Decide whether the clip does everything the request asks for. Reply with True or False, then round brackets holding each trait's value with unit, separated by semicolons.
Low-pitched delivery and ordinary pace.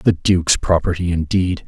True (85 Hz; 145 wpm)